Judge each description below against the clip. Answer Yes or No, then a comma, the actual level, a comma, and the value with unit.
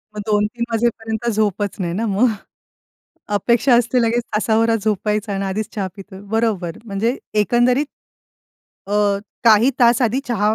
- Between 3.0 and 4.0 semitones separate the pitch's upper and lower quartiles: No, narrow, 2.5 semitones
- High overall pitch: Yes, high, 220 Hz